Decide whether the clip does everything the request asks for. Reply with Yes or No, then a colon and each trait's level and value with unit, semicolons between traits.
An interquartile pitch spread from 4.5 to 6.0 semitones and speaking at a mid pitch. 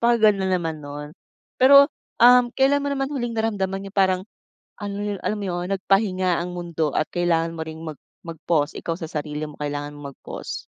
Yes: average, 5.2 semitones; medium, 180 Hz